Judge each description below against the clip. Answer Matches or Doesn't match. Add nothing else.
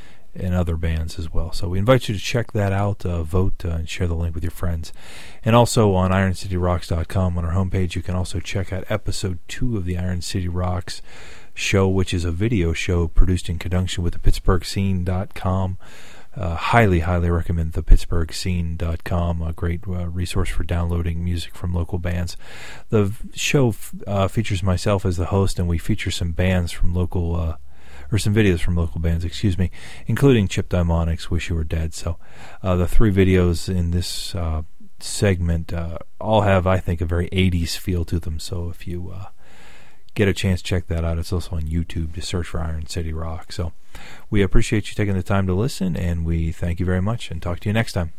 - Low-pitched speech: Matches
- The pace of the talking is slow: Doesn't match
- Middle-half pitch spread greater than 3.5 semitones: Doesn't match